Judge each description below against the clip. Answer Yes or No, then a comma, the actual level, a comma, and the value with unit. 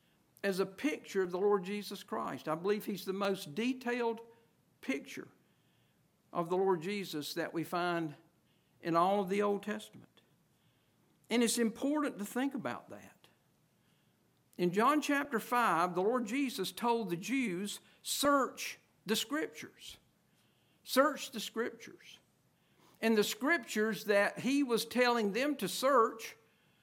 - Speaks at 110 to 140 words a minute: Yes, slow, 135 wpm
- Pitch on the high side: Yes, high, 210 Hz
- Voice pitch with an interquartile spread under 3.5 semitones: No, average, 4.6 semitones